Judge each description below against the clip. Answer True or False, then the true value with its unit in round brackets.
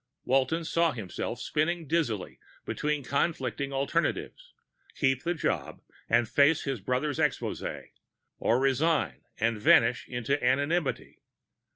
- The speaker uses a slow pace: True (110 wpm)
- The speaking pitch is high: False (140 Hz)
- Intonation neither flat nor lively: True (4.3 semitones)